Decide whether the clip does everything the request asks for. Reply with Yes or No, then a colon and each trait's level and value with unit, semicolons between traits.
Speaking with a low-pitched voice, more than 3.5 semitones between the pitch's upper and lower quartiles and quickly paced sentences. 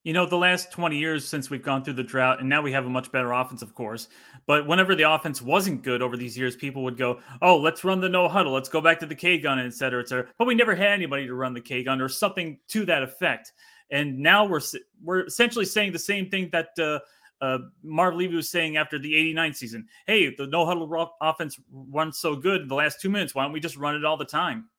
No: medium, 155 Hz; average, 5.0 semitones; fast, 260 wpm